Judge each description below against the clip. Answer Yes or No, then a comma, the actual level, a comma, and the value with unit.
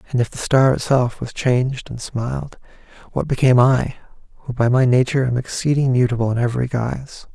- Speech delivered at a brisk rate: No, average, 180 wpm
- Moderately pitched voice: No, low, 125 Hz